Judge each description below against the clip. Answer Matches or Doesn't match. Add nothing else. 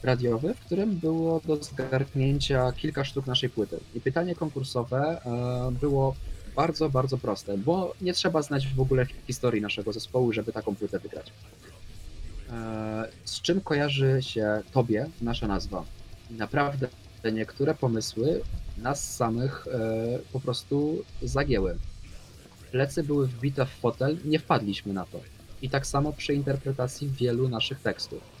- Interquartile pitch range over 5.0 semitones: Doesn't match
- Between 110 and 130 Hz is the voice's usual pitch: Matches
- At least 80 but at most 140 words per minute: Matches